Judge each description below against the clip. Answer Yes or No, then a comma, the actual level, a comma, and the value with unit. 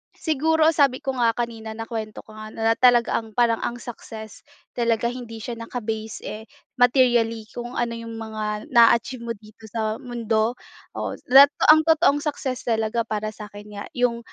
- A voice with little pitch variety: Yes, narrow, 2.1 semitones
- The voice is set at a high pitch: Yes, high, 230 Hz